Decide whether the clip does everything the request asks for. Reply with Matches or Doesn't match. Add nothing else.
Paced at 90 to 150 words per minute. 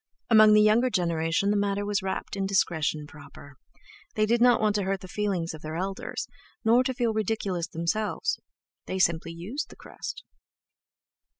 Doesn't match